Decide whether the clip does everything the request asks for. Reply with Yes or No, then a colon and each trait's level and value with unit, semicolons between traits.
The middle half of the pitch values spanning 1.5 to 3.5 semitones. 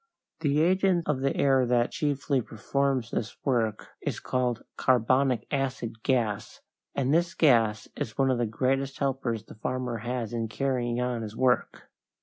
Yes: average, 2.9 semitones